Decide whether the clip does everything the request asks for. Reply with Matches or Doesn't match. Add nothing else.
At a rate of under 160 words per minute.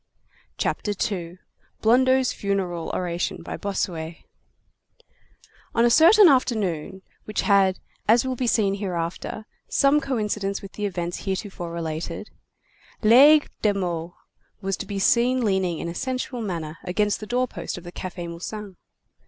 Matches